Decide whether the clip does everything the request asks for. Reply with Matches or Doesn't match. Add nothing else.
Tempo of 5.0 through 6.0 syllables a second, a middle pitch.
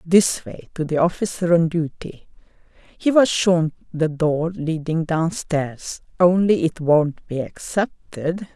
Doesn't match